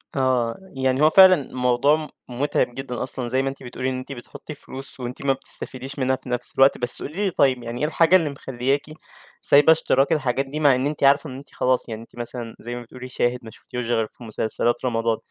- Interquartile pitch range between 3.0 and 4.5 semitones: No, narrow, 2.4 semitones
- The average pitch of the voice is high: No, low, 130 Hz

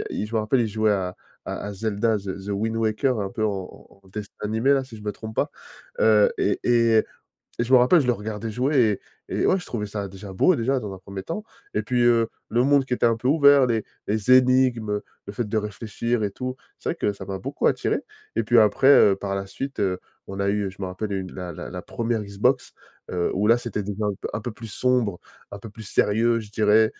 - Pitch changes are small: No, average, 3.1 semitones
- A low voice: Yes, low, 110 Hz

